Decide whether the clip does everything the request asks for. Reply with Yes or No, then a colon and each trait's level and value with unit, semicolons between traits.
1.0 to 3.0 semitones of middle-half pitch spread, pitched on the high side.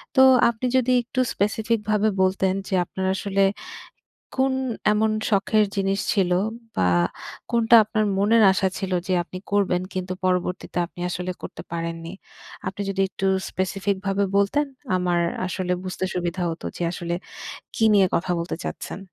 Yes: average, 2.7 semitones; high, 195 Hz